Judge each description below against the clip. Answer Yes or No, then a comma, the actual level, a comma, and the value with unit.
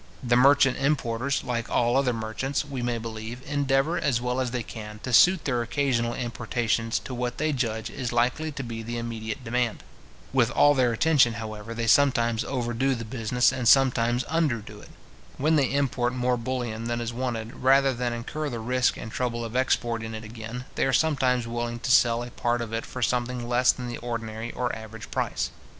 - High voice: No, low, 120 Hz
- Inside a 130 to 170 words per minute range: No, average, 195 wpm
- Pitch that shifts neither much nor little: No, narrow, 2.1 semitones